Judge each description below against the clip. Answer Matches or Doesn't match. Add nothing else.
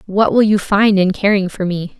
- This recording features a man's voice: Doesn't match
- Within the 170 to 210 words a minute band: Doesn't match